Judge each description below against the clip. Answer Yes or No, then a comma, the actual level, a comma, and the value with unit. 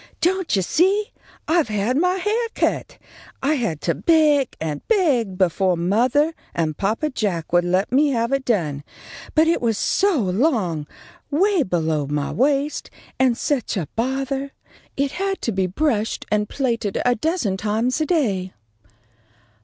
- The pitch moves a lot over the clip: Yes, wide, 8.2 semitones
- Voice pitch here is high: Yes, high, 245 Hz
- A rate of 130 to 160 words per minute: Yes, average, 155 wpm